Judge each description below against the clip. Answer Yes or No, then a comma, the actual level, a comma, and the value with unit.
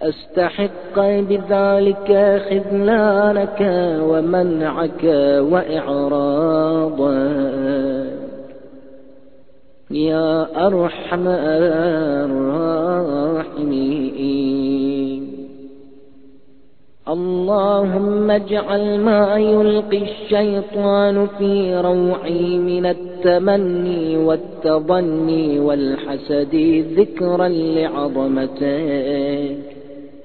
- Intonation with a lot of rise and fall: Yes, wide, 5.7 semitones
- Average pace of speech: No, slow, 40 wpm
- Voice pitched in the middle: Yes, medium, 160 Hz